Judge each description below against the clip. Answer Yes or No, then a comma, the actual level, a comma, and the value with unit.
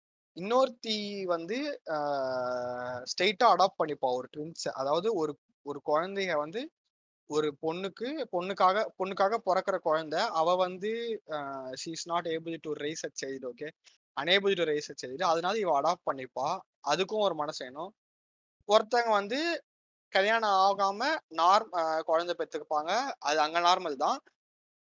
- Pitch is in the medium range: Yes, medium, 175 Hz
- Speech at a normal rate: Yes, average, 120 wpm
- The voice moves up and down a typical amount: No, wide, 5.7 semitones